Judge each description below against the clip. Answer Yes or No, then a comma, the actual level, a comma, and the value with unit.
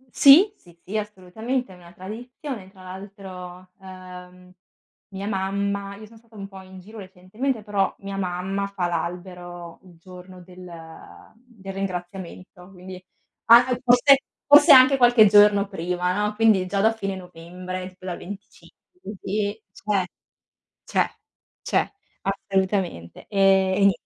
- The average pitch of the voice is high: Yes, high, 195 Hz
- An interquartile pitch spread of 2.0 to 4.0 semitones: Yes, narrow, 2.5 semitones